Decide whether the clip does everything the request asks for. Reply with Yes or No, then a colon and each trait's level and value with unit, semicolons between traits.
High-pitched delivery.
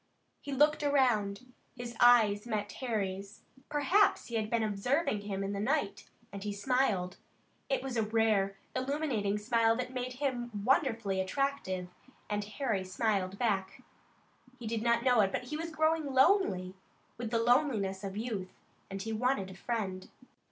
Yes: high, 225 Hz